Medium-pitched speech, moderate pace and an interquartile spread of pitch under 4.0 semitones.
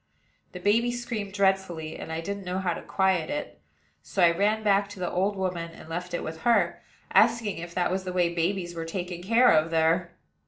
No: medium, 180 Hz; fast, 210 wpm; average, 3.0 semitones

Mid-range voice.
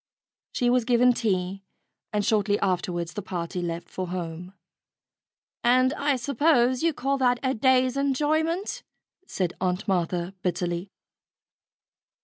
No: high, 215 Hz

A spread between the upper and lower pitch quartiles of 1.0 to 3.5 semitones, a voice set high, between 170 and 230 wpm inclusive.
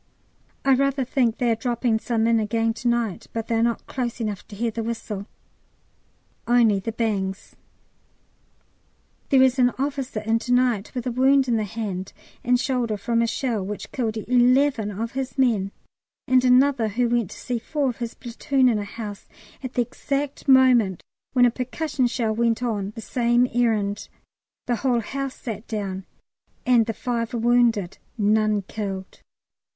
Yes: narrow, 2.5 semitones; high, 235 Hz; average, 175 wpm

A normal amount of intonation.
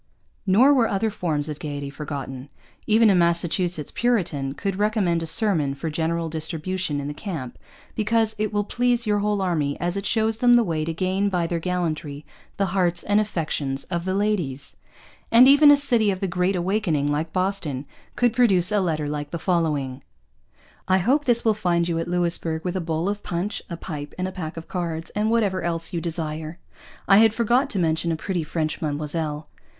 Yes: average, 4.7 semitones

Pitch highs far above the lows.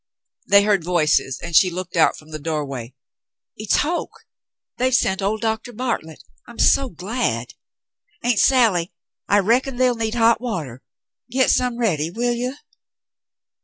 Yes: wide, 6.9 semitones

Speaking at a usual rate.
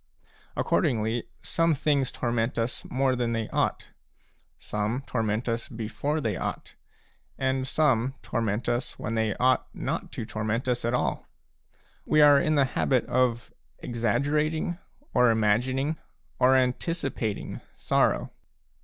No: slow, 125 wpm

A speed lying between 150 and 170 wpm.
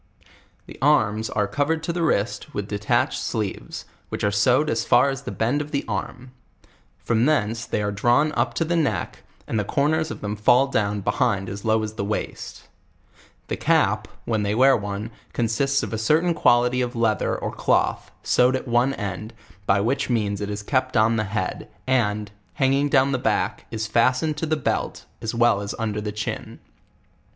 No: average, 195 wpm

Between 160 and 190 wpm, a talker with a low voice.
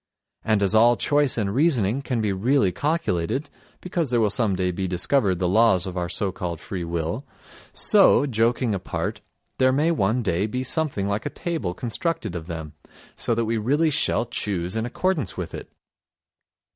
Yes: average, 170 wpm; low, 110 Hz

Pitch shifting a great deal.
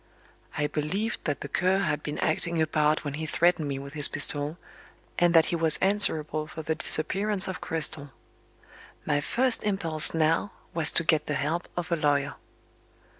No: average, 2.8 semitones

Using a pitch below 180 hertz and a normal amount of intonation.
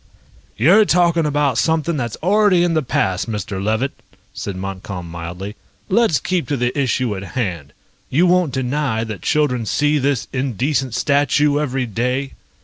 No: low, 135 Hz; wide, 5.7 semitones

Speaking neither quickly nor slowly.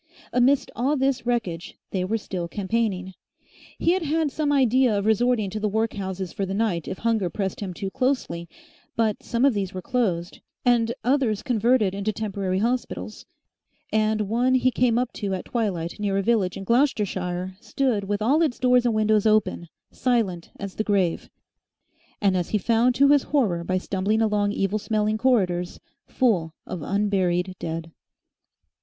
Yes: average, 170 wpm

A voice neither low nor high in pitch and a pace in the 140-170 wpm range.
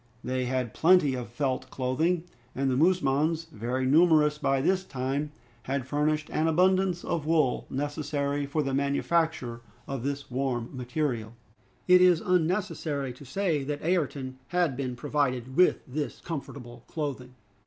Yes: medium, 145 Hz; average, 145 wpm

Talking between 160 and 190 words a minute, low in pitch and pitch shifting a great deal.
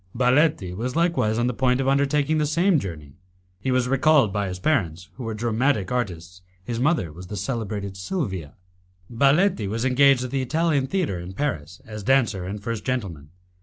Yes: average, 180 wpm; low, 120 Hz; wide, 6.2 semitones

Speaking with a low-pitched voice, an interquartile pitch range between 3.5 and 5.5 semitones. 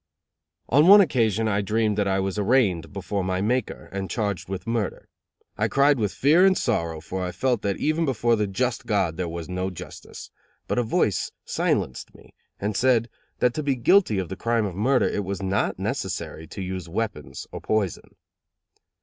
Yes: low, 105 Hz; average, 4.5 semitones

